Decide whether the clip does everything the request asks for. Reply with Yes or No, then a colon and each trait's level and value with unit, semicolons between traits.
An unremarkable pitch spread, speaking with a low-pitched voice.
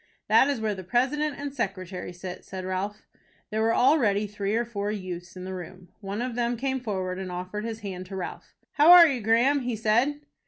No: average, 4.7 semitones; high, 210 Hz